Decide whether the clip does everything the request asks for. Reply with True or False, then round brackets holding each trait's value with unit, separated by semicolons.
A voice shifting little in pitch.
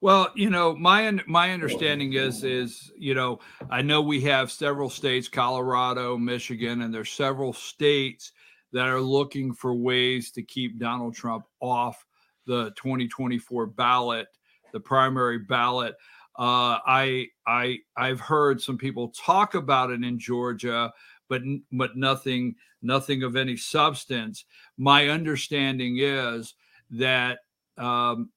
True (2.2 semitones)